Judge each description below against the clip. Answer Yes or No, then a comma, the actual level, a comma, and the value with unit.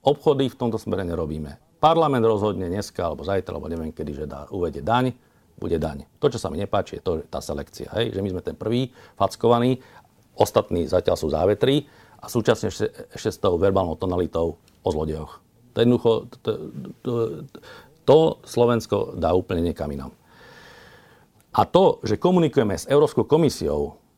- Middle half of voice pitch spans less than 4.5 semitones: No, wide, 6.6 semitones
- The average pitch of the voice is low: Yes, low, 105 Hz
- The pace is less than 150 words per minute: No, average, 160 wpm